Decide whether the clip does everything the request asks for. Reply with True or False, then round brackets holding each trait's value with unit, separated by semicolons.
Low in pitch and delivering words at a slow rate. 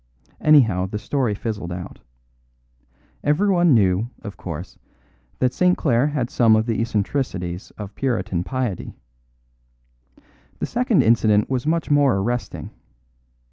True (115 Hz; 120 wpm)